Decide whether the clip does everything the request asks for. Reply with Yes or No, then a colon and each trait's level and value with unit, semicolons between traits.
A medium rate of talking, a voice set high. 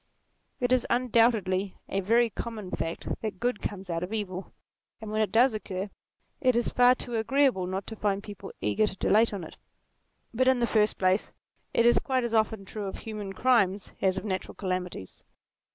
Yes: average, 190 wpm; high, 215 Hz